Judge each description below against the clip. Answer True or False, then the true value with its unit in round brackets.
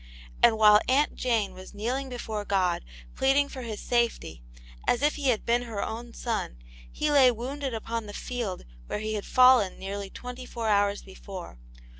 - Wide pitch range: False (3.7 semitones)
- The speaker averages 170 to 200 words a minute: True (175 wpm)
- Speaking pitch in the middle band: False (230 Hz)